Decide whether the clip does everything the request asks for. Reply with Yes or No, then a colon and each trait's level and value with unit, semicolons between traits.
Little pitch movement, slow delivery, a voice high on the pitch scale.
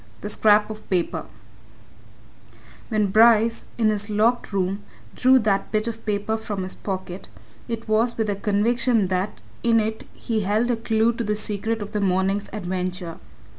No: narrow, 2.3 semitones; average, 165 wpm; high, 215 Hz